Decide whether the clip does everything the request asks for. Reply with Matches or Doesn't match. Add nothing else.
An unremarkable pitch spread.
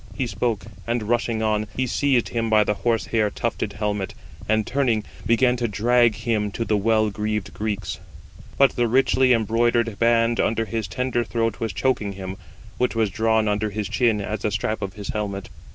Doesn't match